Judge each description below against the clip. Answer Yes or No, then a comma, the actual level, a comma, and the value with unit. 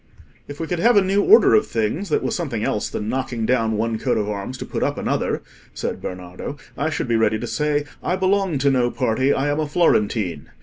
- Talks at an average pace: No, fast, 230 wpm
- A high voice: No, low, 130 Hz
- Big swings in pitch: Yes, wide, 6.7 semitones